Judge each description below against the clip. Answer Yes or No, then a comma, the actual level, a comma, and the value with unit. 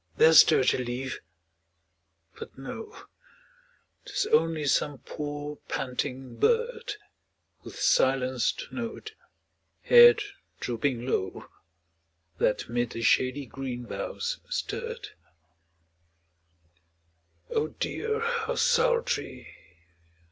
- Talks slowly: Yes, slow, 85 wpm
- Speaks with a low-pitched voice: No, medium, 150 Hz